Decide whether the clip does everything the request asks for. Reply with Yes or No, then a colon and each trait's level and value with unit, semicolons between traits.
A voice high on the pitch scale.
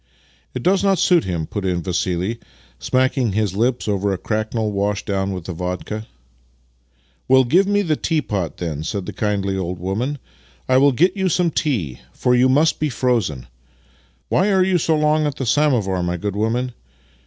No: low, 110 Hz